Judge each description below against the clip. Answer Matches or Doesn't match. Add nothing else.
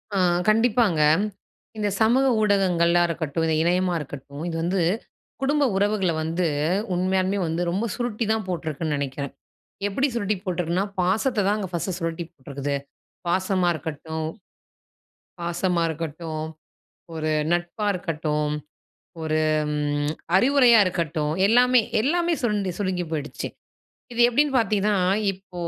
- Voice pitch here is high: Doesn't match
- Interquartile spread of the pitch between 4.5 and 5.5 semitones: Matches